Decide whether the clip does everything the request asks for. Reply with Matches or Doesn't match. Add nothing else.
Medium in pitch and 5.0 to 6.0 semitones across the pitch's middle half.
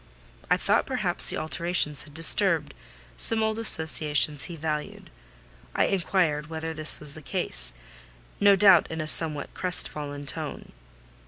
Doesn't match